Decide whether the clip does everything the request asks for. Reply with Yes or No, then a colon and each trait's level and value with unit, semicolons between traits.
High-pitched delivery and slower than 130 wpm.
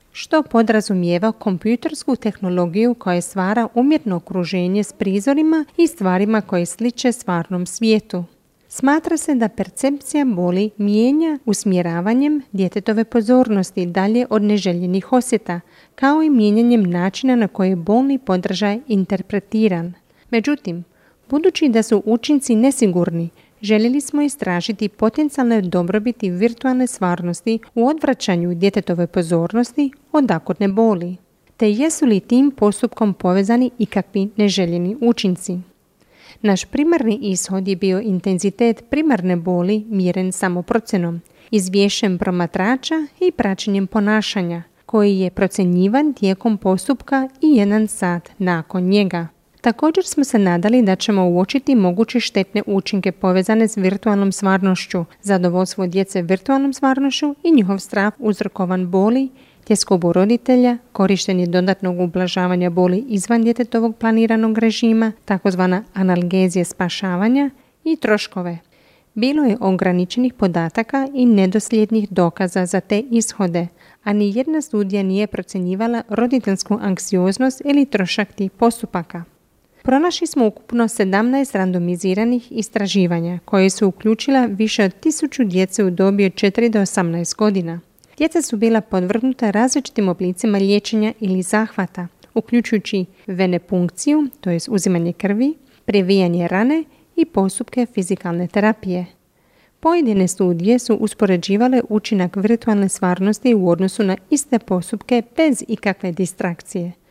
Yes: high, 210 Hz; average, 115 wpm